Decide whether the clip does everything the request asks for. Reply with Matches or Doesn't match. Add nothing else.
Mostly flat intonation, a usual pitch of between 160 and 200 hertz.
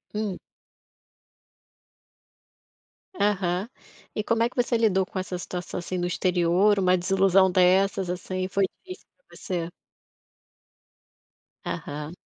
Matches